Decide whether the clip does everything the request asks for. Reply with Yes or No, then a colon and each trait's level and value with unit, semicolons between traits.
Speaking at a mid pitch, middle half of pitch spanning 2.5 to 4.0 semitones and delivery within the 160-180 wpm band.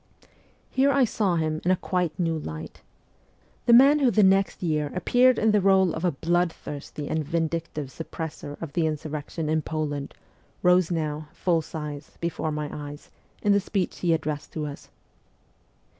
Yes: medium, 165 Hz; average, 3.5 semitones; average, 170 wpm